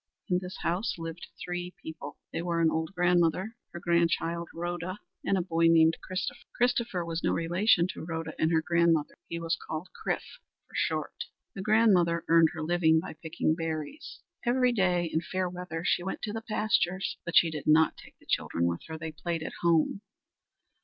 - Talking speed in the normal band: Yes, average, 185 wpm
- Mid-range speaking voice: Yes, medium, 170 Hz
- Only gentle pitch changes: Yes, narrow, 2.1 semitones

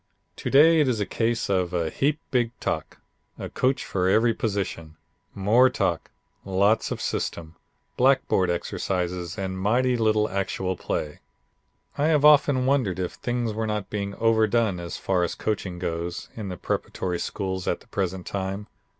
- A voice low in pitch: Yes, low, 100 Hz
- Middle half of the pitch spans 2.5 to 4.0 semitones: No, average, 4.6 semitones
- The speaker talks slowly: No, average, 160 wpm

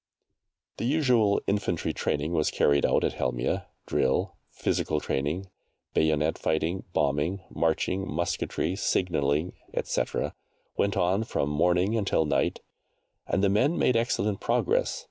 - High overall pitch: No, very low, 90 Hz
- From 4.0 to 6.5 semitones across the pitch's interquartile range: Yes, average, 4.8 semitones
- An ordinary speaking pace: No, slow, 125 wpm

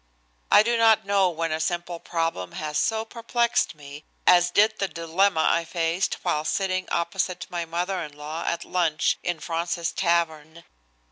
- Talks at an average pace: Yes, average, 160 wpm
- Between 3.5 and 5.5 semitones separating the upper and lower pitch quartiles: No, average, 2.9 semitones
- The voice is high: No, medium, 170 Hz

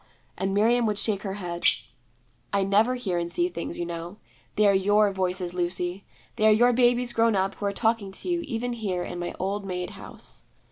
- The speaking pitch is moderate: No, high, 200 Hz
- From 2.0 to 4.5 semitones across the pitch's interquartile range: Yes, average, 3.8 semitones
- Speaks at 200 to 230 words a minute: Yes, fast, 205 wpm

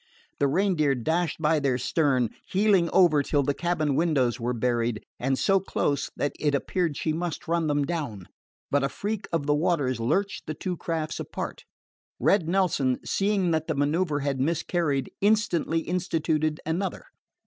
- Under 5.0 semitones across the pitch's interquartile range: Yes, average, 3.8 semitones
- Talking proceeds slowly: No, average, 160 wpm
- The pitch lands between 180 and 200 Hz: No, medium, 155 Hz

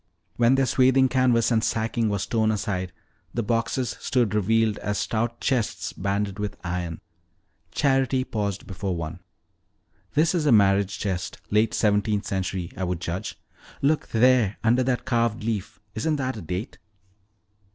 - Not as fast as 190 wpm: Yes, average, 150 wpm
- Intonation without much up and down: No, average, 4.0 semitones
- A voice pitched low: Yes, low, 110 Hz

